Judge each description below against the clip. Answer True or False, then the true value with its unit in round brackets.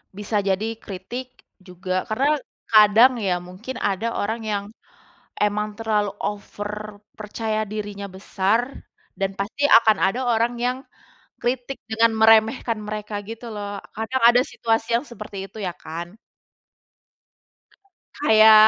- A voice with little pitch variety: True (2.2 semitones)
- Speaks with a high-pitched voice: True (215 Hz)